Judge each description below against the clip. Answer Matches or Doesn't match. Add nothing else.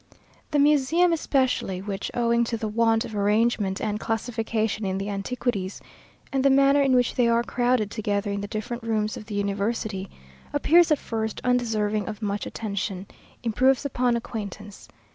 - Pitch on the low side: Doesn't match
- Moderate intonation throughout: Matches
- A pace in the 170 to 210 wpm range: Doesn't match